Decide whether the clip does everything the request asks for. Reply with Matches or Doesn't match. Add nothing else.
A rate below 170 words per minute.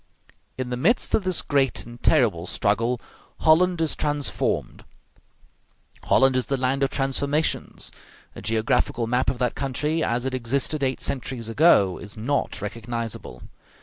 Matches